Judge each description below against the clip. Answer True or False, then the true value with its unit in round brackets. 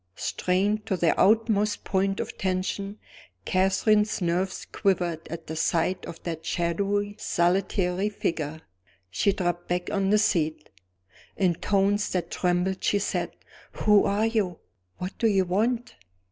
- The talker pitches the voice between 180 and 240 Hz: True (190 Hz)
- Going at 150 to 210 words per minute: False (135 wpm)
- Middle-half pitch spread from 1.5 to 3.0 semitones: True (2.6 semitones)